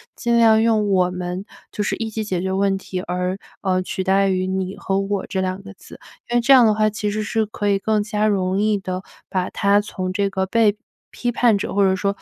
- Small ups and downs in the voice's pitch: Yes, narrow, 2.2 semitones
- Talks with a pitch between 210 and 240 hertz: No, high, 200 Hz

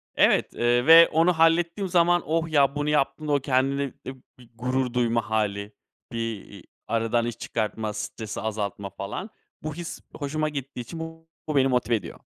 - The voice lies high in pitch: No, low, 135 Hz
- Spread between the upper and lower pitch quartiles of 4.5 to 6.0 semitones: Yes, wide, 5.6 semitones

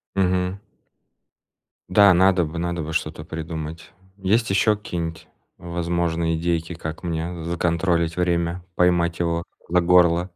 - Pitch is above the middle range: No, very low, 85 Hz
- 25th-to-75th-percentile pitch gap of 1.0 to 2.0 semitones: Yes, narrow, 1.5 semitones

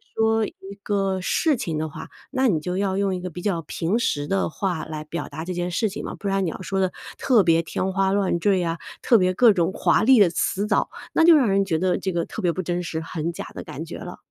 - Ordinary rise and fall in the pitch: Yes, average, 3.0 semitones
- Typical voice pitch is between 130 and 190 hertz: Yes, medium, 185 Hz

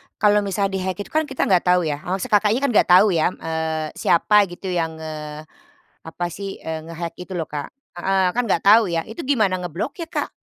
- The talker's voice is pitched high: No, medium, 180 Hz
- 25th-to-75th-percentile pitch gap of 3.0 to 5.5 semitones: Yes, average, 4.1 semitones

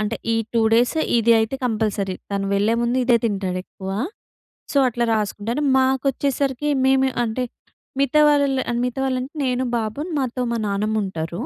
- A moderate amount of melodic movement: Yes, average, 3.8 semitones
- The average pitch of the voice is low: No, high, 235 Hz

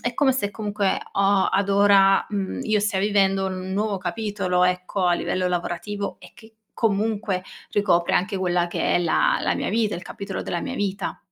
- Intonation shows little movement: Yes, narrow, 2.1 semitones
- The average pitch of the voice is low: No, high, 195 Hz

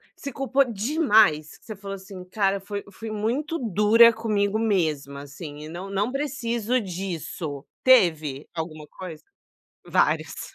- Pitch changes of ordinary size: No, wide, 5.8 semitones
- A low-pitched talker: No, high, 200 Hz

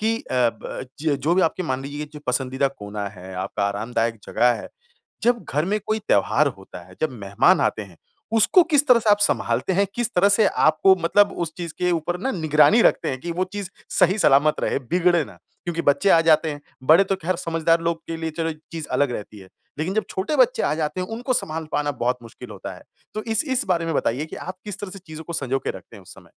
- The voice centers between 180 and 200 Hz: No, medium, 165 Hz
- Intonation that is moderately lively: No, wide, 5.9 semitones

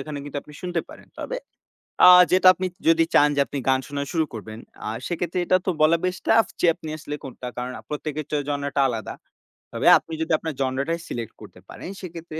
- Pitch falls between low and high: Yes, medium, 155 Hz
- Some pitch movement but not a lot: Yes, average, 3.6 semitones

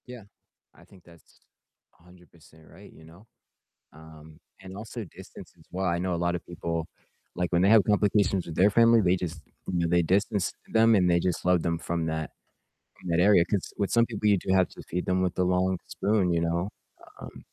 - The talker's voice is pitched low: Yes, very low, 90 Hz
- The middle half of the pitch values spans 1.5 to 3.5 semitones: Yes, average, 2.9 semitones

